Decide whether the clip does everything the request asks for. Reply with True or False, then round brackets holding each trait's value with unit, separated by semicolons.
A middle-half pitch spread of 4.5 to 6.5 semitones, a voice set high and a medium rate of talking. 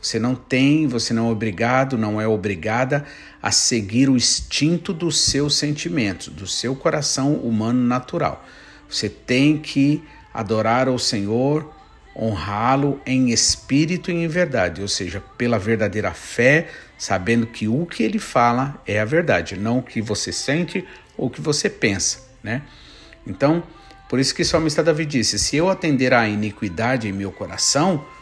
False (5.1 semitones; 125 Hz; 155 wpm)